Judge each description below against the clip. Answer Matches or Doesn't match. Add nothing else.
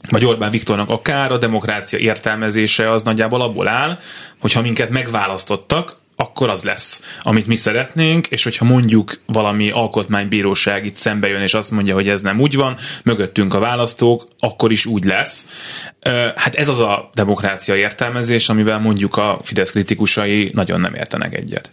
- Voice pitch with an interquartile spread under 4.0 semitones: Matches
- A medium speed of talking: Doesn't match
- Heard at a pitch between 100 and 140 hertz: Matches